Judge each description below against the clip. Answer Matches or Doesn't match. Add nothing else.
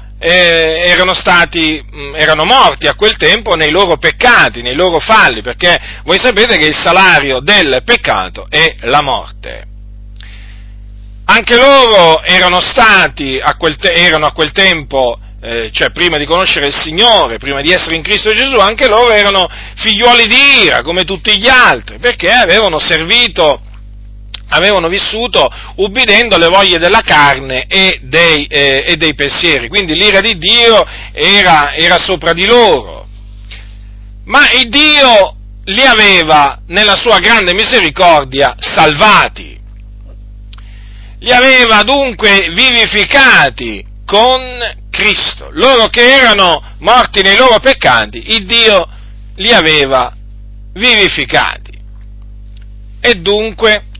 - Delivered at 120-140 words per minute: Matches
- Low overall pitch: Doesn't match